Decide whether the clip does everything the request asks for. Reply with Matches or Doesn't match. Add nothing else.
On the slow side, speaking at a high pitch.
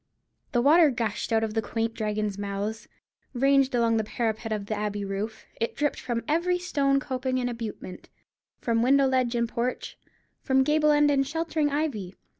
Doesn't match